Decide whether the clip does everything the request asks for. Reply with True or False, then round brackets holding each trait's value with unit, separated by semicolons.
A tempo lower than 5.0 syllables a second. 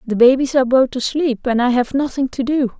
False (5.6 syllables/s)